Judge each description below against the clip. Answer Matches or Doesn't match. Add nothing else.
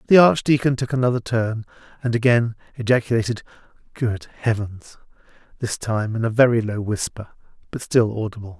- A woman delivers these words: Doesn't match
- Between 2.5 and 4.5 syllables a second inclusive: Doesn't match